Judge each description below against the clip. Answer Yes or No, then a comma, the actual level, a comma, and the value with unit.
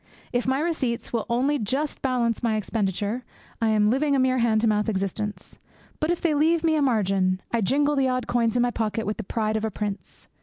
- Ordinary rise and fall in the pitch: Yes, average, 4.0 semitones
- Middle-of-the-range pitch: No, high, 235 Hz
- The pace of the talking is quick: Yes, fast, 225 wpm